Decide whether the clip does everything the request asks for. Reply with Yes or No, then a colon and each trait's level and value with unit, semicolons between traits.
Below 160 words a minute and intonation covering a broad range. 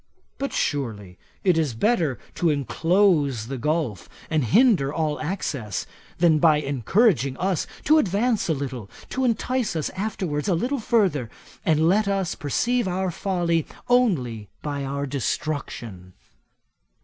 Yes: slow, 135 wpm; wide, 6.3 semitones